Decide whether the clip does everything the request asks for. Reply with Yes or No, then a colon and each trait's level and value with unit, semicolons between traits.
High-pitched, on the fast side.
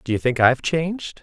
No: medium, 140 Hz; fast, 245 wpm